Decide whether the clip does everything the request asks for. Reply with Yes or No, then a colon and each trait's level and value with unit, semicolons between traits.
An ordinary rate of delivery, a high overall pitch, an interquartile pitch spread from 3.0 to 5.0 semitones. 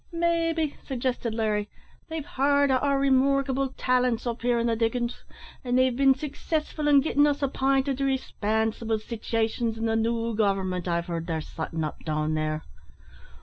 Yes: average, 160 wpm; high, 245 Hz; average, 3.9 semitones